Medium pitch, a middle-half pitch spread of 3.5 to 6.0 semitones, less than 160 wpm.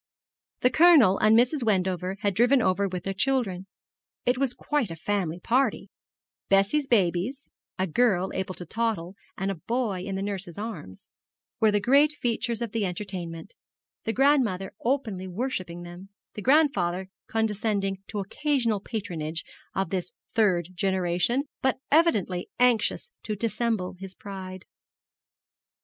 No: high, 200 Hz; average, 4.5 semitones; average, 140 wpm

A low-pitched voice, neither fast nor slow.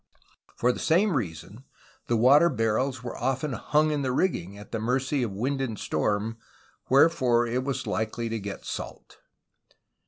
Yes: low, 125 Hz; average, 160 wpm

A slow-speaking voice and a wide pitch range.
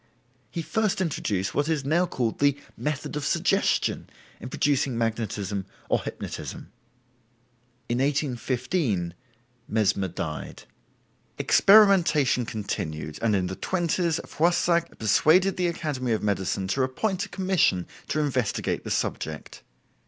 Yes: slow, 120 wpm; wide, 8.2 semitones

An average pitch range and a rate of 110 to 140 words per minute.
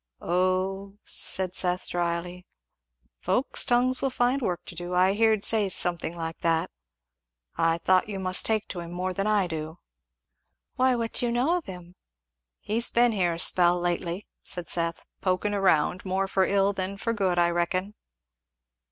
No: average, 3.1 semitones; average, 170 wpm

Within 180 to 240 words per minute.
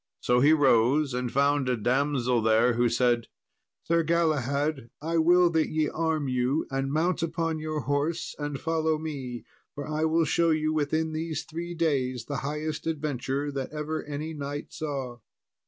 No: average, 165 wpm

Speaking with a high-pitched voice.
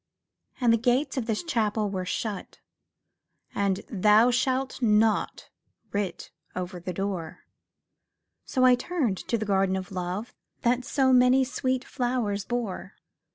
Yes: high, 220 Hz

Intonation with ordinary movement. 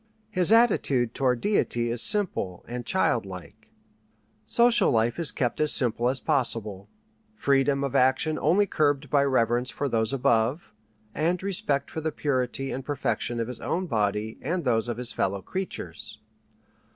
Yes: average, 5.0 semitones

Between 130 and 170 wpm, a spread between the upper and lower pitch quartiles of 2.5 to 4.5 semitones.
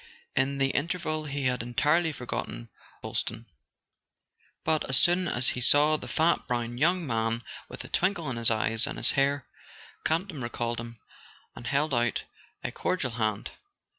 No: average, 160 wpm; average, 4.9 semitones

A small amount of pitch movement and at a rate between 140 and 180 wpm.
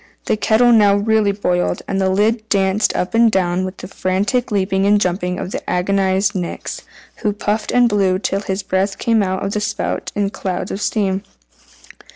No: narrow, 1.9 semitones; average, 190 wpm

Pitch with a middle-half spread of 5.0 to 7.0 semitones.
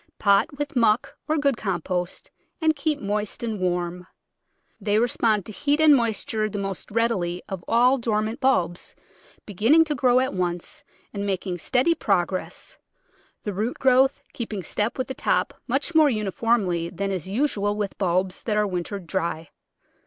Yes: wide, 5.4 semitones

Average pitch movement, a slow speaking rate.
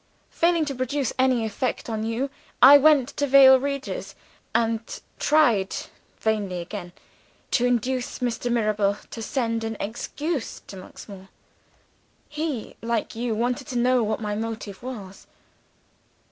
Yes: average, 3.4 semitones; slow, 130 wpm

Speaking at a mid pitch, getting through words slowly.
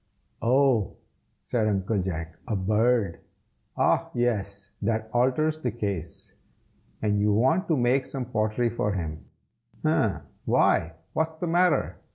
No: low, 110 Hz; slow, 130 wpm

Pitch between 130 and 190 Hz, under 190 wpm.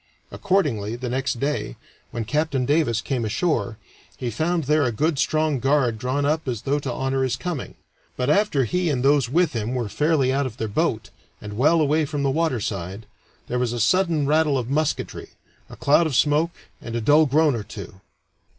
No: low, 135 Hz; average, 195 wpm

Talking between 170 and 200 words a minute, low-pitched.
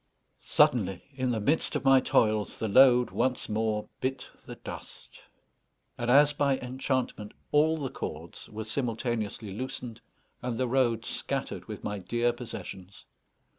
No: average, 140 wpm; low, 120 Hz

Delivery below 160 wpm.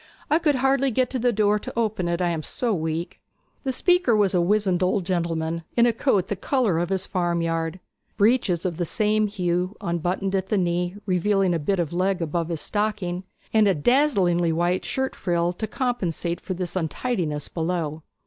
No: average, 190 wpm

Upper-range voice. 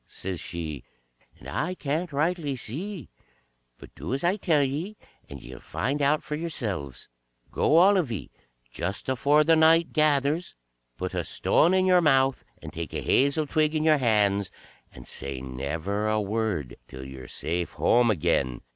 No: low, 135 Hz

